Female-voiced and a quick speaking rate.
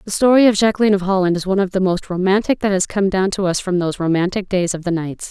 Yes: female; fast, 285 wpm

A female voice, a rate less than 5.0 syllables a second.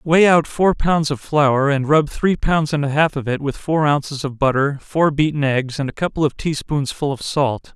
No: male; 4.7 syllables/s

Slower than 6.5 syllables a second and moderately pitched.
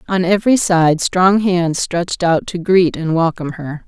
Yes: 4.6 syllables/s; medium, 175 Hz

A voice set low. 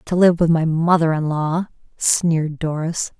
No: medium, 165 Hz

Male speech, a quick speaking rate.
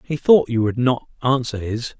Yes: male; fast, 210 wpm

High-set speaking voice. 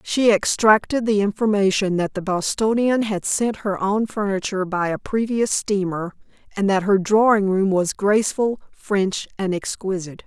Yes: high, 200 Hz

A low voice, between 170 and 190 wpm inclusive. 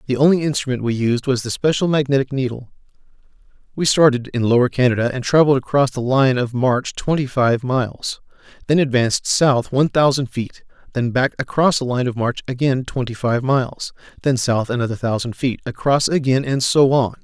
Yes: low, 130 Hz; average, 180 wpm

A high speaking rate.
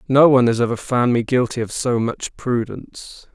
No: average, 195 wpm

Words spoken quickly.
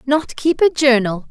No: average, 185 wpm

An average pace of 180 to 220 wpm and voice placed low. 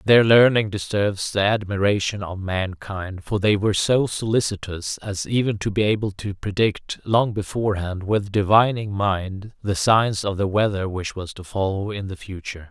No: average, 170 wpm; low, 100 Hz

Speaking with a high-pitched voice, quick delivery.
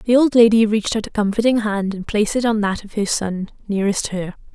Yes: high, 210 Hz; fast, 240 wpm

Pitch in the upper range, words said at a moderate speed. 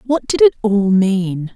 Yes: high, 215 Hz; average, 195 wpm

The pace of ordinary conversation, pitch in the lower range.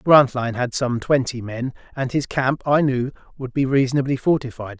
Yes: average, 175 wpm; low, 130 Hz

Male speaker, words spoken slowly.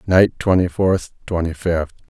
Yes: male; slow, 110 wpm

